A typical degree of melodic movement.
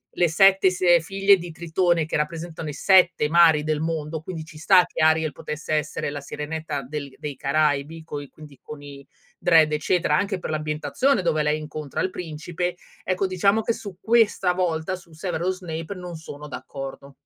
Yes: average, 3.0 semitones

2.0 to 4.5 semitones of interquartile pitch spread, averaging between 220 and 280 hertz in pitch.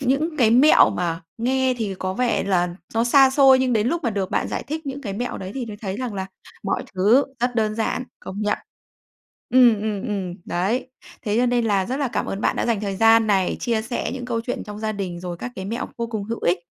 Yes: average, 4.0 semitones; high, 225 Hz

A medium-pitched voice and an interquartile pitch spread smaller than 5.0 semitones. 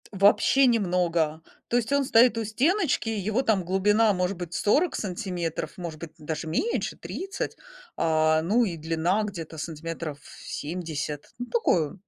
No: medium, 180 Hz; wide, 5.5 semitones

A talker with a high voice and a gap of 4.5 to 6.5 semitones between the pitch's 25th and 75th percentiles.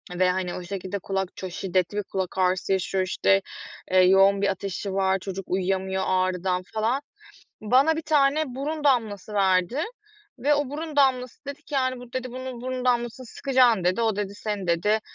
Yes: high, 205 Hz; wide, 5.4 semitones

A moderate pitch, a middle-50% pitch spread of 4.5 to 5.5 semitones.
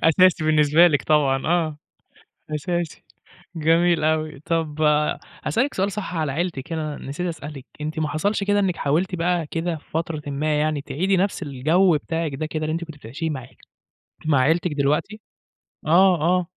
No: medium, 160 Hz; average, 2.8 semitones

